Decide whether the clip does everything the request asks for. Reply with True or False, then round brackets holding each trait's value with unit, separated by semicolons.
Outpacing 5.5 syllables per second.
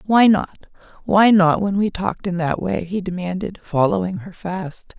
False (4.7 syllables/s)